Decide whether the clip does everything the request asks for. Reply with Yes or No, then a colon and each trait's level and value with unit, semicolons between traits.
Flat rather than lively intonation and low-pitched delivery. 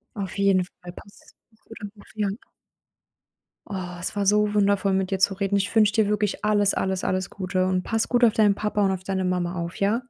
No: narrow, 2.0 semitones; high, 200 Hz